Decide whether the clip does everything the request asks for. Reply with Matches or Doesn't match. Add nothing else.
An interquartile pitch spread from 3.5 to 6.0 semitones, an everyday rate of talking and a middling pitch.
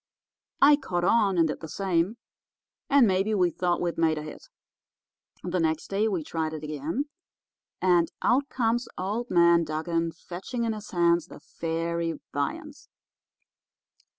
Matches